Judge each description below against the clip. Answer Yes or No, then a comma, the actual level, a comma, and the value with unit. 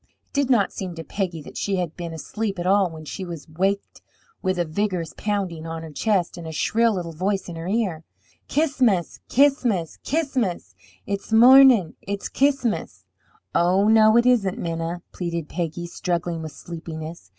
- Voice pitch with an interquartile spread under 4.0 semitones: No, average, 4.5 semitones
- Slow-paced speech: No, average, 170 wpm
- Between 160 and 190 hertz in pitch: Yes, medium, 185 Hz